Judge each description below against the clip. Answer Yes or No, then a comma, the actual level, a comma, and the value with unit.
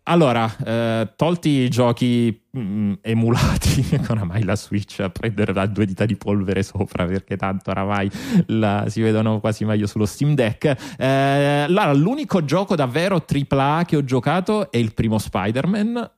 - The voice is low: Yes, low, 115 Hz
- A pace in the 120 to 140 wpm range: No, average, 165 wpm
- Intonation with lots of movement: Yes, wide, 5.7 semitones